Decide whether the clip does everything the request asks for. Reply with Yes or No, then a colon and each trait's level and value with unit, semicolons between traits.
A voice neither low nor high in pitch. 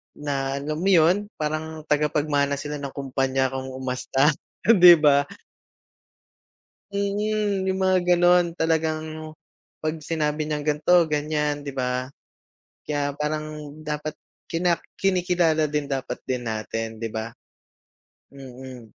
Yes: medium, 150 Hz